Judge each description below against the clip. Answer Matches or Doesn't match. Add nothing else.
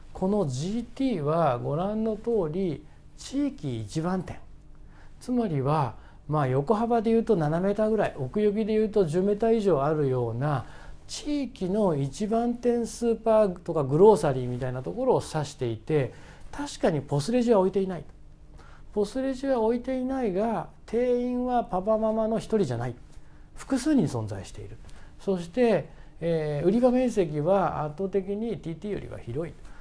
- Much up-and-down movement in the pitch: Matches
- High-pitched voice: Matches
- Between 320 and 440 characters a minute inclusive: Doesn't match